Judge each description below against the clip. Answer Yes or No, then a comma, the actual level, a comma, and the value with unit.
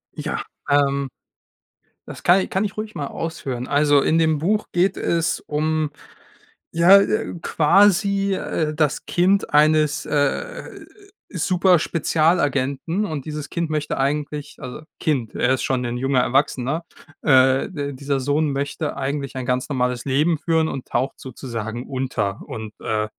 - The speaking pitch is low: No, medium, 150 Hz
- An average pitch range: Yes, average, 3.7 semitones